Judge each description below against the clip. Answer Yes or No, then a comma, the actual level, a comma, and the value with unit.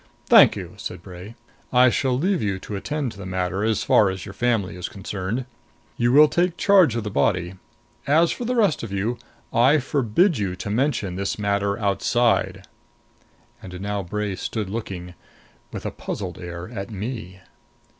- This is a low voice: Yes, low, 105 Hz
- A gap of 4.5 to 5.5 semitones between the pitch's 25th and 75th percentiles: Yes, average, 4.9 semitones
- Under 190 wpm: Yes, average, 175 wpm